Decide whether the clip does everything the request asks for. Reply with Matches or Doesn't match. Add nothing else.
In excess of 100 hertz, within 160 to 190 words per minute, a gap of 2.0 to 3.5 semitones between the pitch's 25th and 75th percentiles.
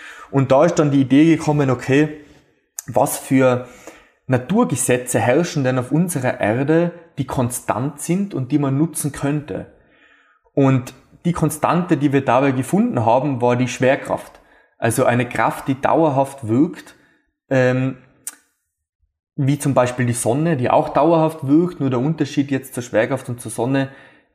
Doesn't match